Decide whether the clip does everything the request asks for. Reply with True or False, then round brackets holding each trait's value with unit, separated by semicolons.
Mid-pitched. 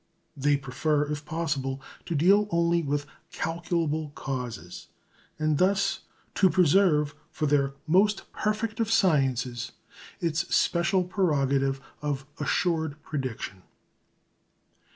True (155 Hz)